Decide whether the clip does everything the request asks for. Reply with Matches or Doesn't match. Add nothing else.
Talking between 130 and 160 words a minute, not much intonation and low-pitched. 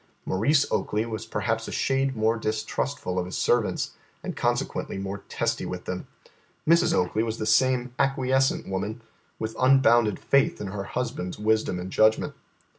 Doesn't match